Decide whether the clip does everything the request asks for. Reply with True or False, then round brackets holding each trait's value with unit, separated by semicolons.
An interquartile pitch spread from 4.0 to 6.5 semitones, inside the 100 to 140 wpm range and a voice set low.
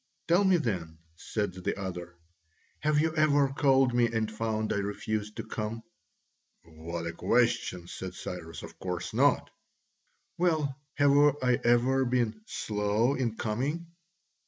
True (5.3 semitones; 135 wpm; 115 Hz)